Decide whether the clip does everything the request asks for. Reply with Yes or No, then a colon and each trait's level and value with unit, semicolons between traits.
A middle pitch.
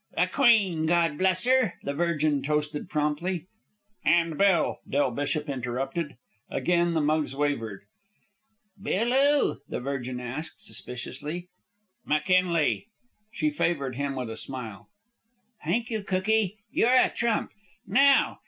Yes: medium, 160 Hz